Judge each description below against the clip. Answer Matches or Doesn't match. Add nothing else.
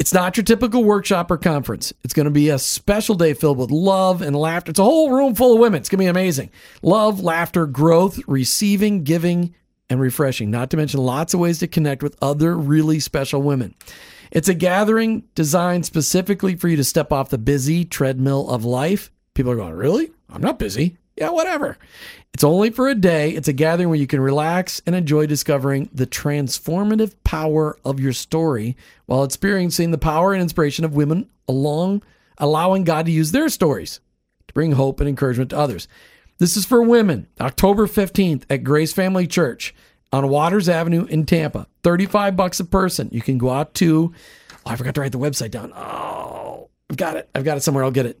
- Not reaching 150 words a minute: Doesn't match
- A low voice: Doesn't match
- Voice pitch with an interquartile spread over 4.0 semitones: Matches